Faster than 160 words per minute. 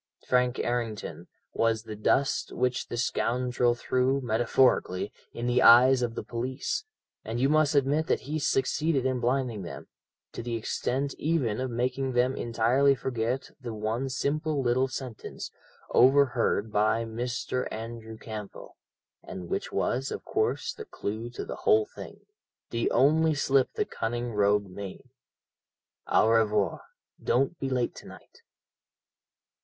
No: average, 140 wpm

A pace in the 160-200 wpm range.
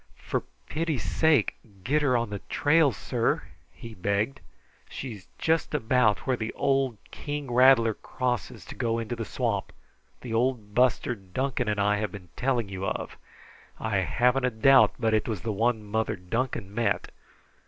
Yes: average, 165 wpm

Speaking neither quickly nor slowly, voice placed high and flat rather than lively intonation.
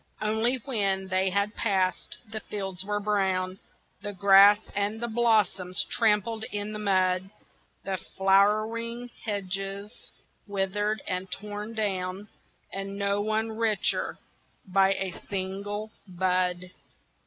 No: slow, 110 wpm; high, 200 Hz; narrow, 1.9 semitones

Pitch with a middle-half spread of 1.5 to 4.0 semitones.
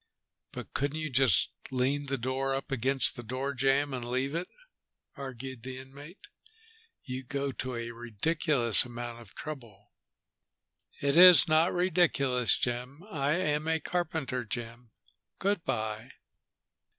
Yes: average, 3.6 semitones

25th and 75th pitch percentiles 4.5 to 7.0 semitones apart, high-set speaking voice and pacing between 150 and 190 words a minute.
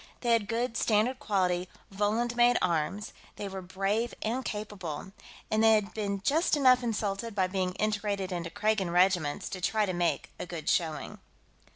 No: average, 3.5 semitones; high, 205 Hz; average, 170 wpm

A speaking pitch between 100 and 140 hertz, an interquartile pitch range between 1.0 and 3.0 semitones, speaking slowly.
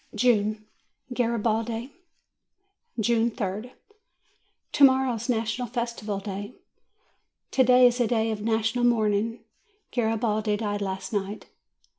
No: high, 225 Hz; narrow, 2.4 semitones; slow, 115 wpm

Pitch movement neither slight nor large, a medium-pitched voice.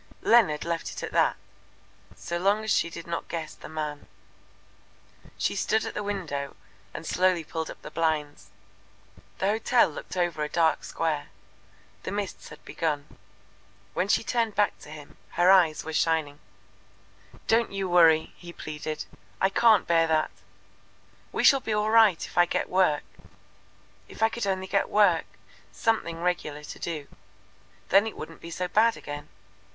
Yes: average, 4.4 semitones; medium, 170 Hz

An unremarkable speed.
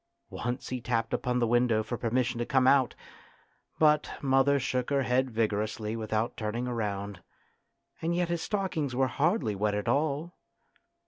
Yes: average, 155 wpm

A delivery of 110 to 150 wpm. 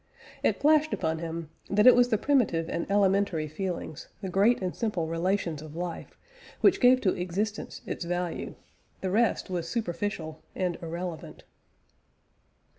Yes: average, 145 wpm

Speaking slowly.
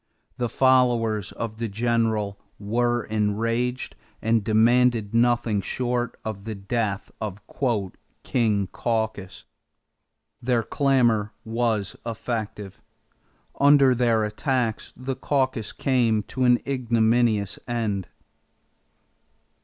Yes: slow, 95 wpm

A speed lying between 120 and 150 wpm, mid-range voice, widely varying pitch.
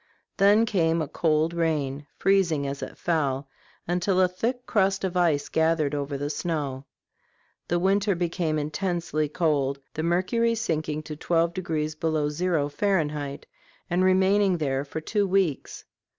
No: average, 145 wpm; medium, 165 Hz; average, 3.8 semitones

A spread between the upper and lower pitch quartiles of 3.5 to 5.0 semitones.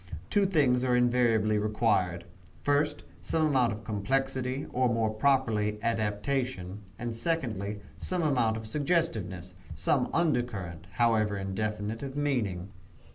Yes: average, 4.3 semitones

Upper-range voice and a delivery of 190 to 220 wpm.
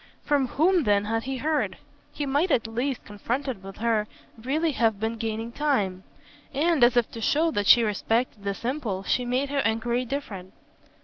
No: high, 240 Hz; average, 180 wpm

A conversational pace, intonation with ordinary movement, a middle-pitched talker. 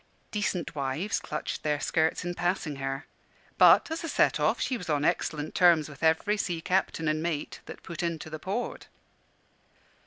Yes: average, 175 wpm; average, 3.3 semitones; medium, 165 Hz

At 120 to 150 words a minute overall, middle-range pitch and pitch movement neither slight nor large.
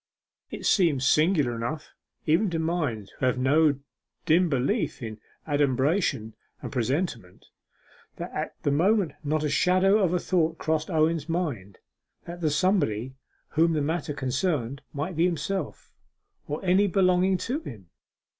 Yes: average, 145 wpm; medium, 155 Hz; average, 5.0 semitones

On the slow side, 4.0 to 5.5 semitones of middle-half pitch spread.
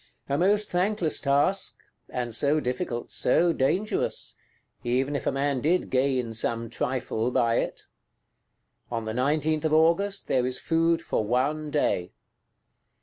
Yes: slow, 130 wpm; average, 4.8 semitones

